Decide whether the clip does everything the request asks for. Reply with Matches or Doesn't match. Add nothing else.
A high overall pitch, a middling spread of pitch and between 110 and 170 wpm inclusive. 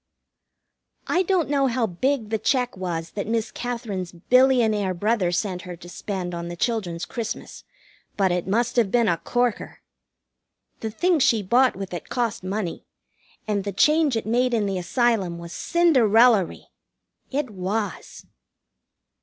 Matches